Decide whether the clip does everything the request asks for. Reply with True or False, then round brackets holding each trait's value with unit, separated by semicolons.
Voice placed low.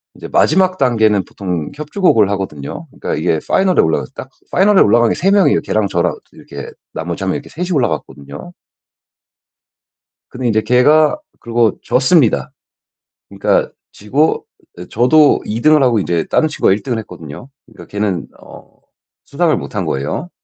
True (115 Hz)